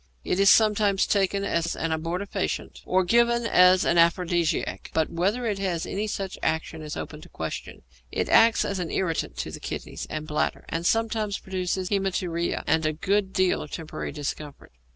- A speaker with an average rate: Yes, average, 175 wpm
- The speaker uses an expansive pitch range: No, average, 3.3 semitones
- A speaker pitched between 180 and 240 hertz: Yes, medium, 185 Hz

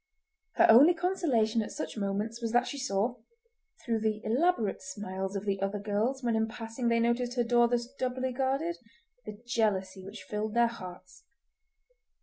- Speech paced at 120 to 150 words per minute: No, average, 165 wpm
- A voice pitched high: Yes, high, 230 Hz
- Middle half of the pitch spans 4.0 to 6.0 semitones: No, average, 3.0 semitones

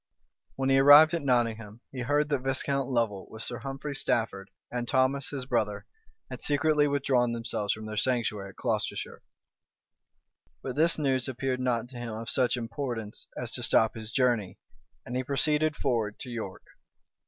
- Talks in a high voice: No, low, 125 Hz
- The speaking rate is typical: Yes, average, 165 wpm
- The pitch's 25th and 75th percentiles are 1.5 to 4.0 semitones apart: Yes, average, 3.5 semitones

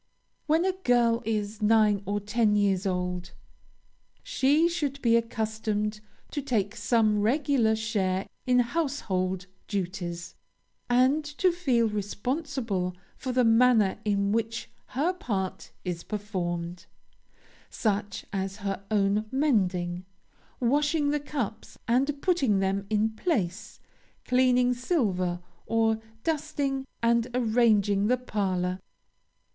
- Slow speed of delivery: Yes, slow, 110 wpm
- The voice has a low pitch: No, high, 220 Hz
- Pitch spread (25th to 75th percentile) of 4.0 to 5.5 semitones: Yes, average, 4.4 semitones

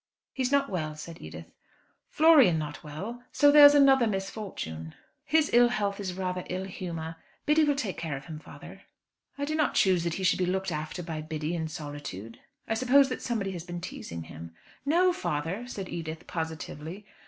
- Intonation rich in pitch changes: Yes, wide, 7.6 semitones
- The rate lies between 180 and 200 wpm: Yes, average, 185 wpm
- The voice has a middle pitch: Yes, medium, 180 Hz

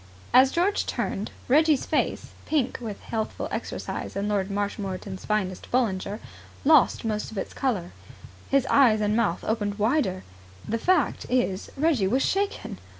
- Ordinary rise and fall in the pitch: Yes, average, 5.0 semitones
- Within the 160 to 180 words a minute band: No, average, 150 wpm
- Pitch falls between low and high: No, high, 220 Hz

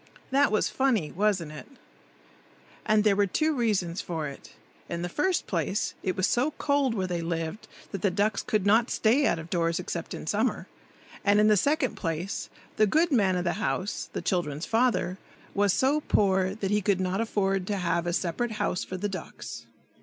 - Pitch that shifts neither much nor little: Yes, average, 3.9 semitones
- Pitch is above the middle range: Yes, high, 200 Hz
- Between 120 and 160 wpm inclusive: No, average, 195 wpm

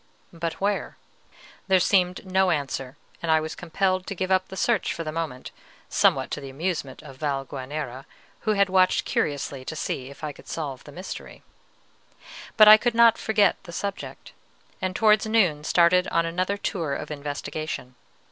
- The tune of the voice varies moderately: Yes, average, 4.6 semitones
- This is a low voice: No, medium, 170 Hz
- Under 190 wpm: Yes, average, 170 wpm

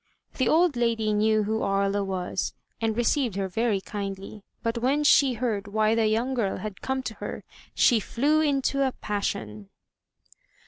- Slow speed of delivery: No, average, 165 wpm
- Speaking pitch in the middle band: No, high, 220 Hz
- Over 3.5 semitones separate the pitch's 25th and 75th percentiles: Yes, average, 4.1 semitones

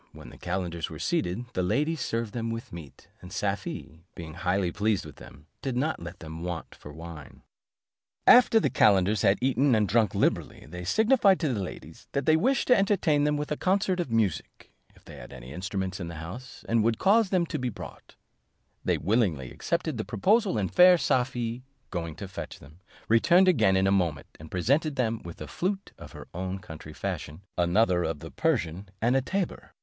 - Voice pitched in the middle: No, low, 110 Hz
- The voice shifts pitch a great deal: Yes, wide, 8.9 semitones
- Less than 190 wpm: No, average, 200 wpm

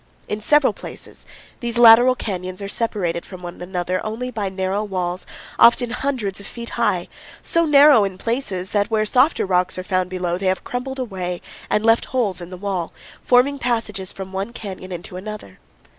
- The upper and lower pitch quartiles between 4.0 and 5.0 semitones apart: Yes, average, 4.5 semitones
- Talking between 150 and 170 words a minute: No, average, 180 wpm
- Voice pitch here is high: Yes, high, 200 Hz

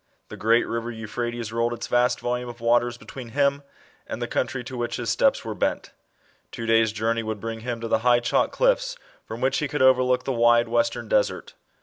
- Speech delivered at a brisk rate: Yes, fast, 215 wpm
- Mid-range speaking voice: No, low, 120 Hz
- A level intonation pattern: Yes, narrow, 2.0 semitones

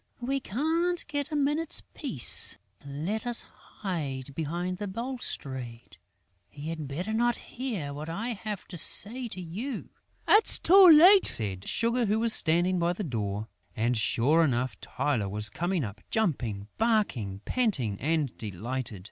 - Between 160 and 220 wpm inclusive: No, average, 150 wpm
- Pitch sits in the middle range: Yes, medium, 175 Hz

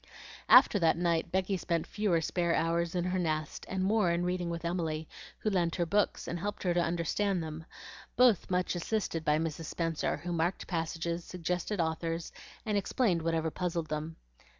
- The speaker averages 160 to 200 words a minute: Yes, average, 175 wpm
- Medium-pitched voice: Yes, medium, 170 Hz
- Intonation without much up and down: Yes, narrow, 1.9 semitones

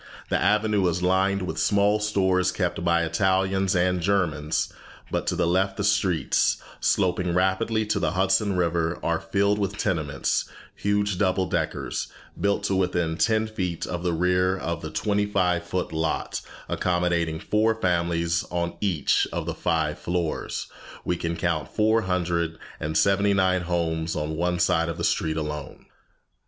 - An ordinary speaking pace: Yes, average, 160 wpm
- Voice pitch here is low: Yes, very low, 90 Hz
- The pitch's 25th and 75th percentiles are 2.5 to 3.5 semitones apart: Yes, average, 2.8 semitones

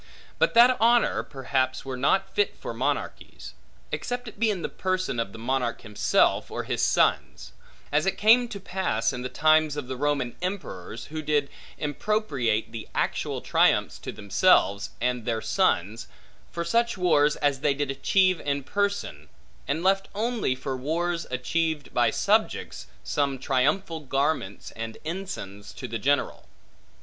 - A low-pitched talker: No, medium, 145 Hz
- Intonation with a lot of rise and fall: Yes, wide, 6.9 semitones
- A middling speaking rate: Yes, average, 155 wpm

